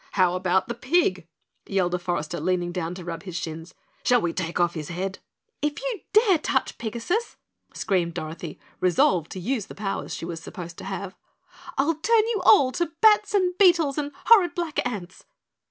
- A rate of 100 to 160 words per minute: No, average, 185 wpm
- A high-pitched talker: Yes, high, 195 Hz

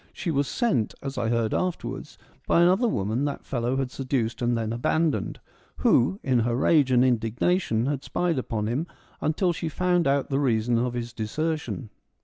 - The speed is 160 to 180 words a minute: Yes, average, 175 wpm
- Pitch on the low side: Yes, low, 130 Hz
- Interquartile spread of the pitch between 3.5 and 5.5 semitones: Yes, average, 5.2 semitones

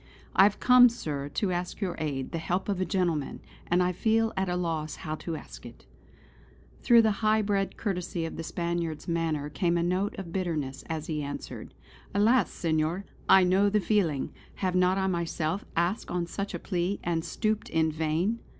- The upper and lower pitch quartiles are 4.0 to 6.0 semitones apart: No, average, 3.4 semitones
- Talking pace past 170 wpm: Yes, average, 190 wpm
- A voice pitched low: No, medium, 180 Hz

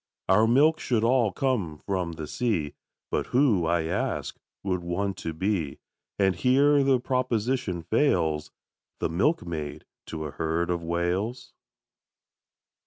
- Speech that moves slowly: Yes, slow, 130 wpm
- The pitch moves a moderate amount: No, wide, 7.0 semitones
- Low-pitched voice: Yes, very low, 95 Hz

